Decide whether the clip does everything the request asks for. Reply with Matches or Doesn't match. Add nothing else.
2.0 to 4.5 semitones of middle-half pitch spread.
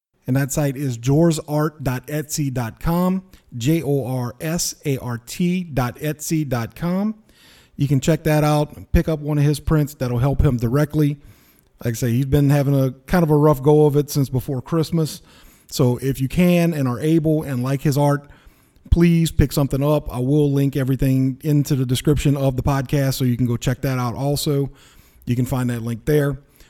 Matches